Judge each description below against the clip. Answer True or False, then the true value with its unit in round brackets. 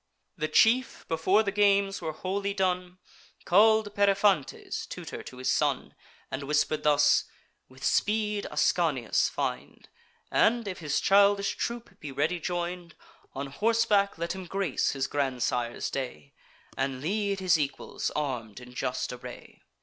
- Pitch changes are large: True (6.4 semitones)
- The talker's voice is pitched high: False (180 Hz)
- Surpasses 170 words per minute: False (135 wpm)